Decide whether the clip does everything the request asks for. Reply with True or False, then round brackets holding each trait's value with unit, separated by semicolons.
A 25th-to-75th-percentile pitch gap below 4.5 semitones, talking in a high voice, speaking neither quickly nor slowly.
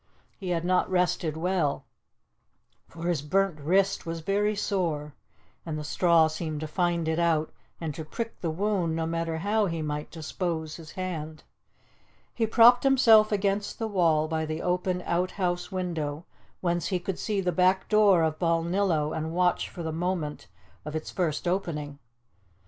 False (3.0 semitones; 170 Hz; 165 wpm)